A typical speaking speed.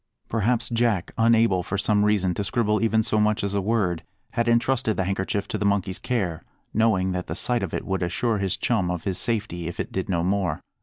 No: fast, 220 wpm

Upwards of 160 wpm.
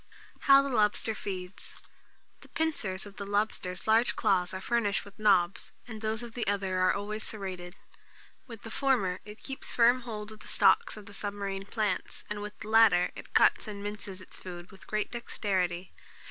Yes: average, 180 wpm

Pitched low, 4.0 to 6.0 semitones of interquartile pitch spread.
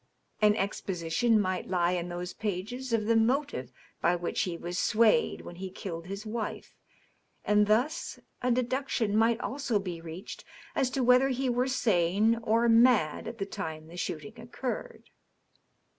No: high, 215 Hz; average, 5.2 semitones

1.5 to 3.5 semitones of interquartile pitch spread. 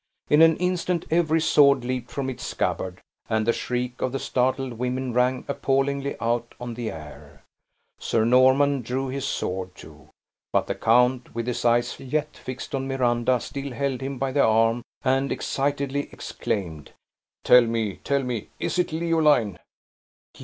Yes: average, 2.8 semitones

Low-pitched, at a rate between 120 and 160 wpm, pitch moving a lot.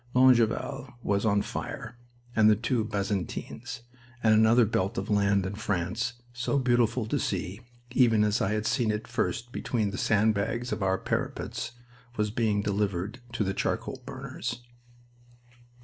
No: low, 110 Hz; average, 150 wpm; average, 3.0 semitones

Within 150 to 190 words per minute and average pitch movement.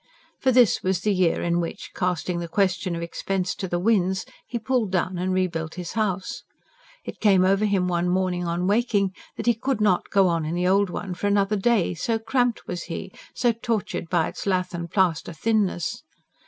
No: average, 200 wpm; average, 3.0 semitones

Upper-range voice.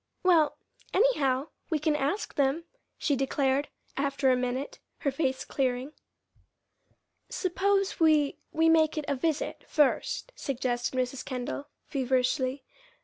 Yes: very high, 280 Hz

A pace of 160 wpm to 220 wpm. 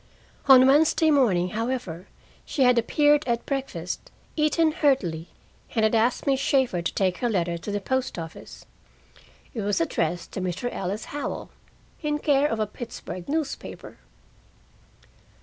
No: average, 145 wpm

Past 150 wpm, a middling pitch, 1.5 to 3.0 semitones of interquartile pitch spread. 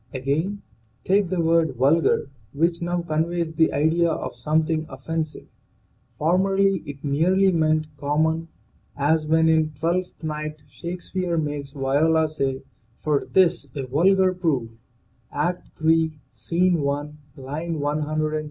No: slow, 135 wpm; medium, 160 Hz; average, 2.7 semitones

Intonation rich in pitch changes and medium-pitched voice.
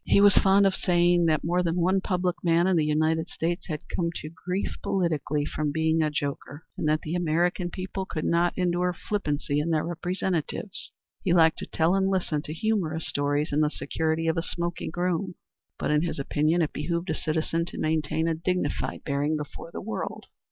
No: narrow, 2.6 semitones; medium, 165 Hz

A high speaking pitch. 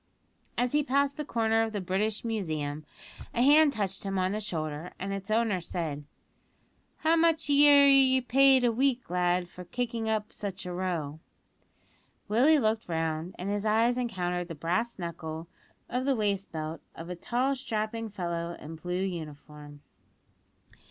Yes: high, 205 Hz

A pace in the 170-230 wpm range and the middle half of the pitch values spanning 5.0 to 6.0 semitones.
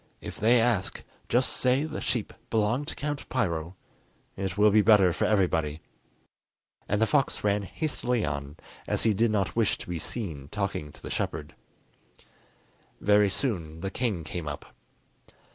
No: average, 160 wpm; average, 5.3 semitones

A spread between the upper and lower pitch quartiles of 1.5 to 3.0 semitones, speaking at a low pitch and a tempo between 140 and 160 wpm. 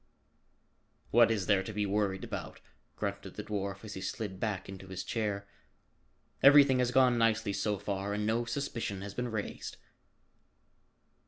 Yes: narrow, 2.6 semitones; low, 105 Hz; average, 155 wpm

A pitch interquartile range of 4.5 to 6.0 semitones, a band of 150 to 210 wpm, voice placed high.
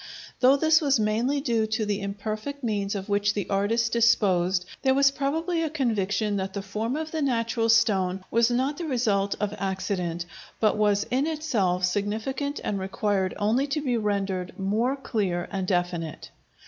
Yes: average, 5.0 semitones; average, 170 wpm; high, 215 Hz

